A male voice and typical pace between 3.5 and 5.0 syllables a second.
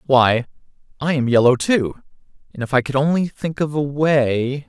Yes: male; 4.6 syllables/s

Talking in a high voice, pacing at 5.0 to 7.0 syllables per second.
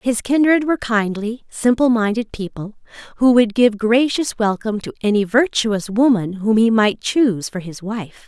No: high, 225 Hz; 4.7 syllables/s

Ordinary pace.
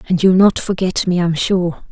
No: fast, 220 wpm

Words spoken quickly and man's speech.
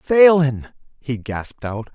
No: slow, 125 wpm; male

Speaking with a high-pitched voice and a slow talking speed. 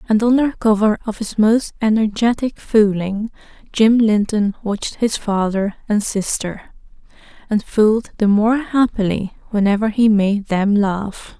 Yes: high, 215 Hz; slow, 130 wpm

